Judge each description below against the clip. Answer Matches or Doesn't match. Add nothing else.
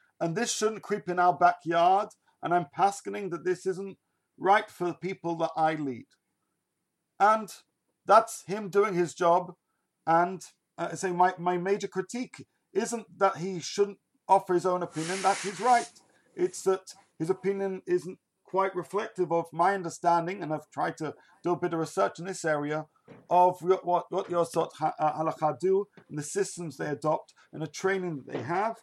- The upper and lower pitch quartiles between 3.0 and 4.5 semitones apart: Doesn't match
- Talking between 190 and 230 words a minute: Doesn't match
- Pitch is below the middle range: Doesn't match